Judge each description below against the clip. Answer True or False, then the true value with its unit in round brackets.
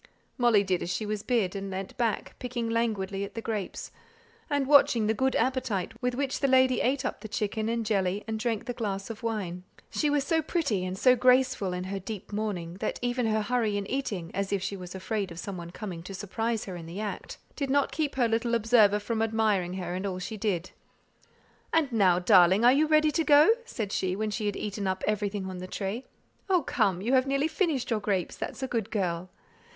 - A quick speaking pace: True (225 wpm)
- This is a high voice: True (215 Hz)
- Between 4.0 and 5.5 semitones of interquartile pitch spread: True (4.4 semitones)